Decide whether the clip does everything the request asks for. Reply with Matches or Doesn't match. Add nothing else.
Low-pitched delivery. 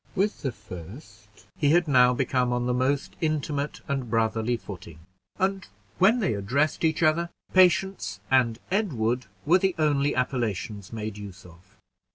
Matches